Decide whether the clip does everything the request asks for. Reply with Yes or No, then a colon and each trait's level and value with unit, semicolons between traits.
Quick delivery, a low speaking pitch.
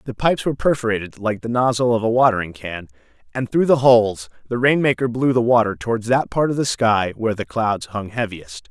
Yes: fast, 220 wpm; low, 115 Hz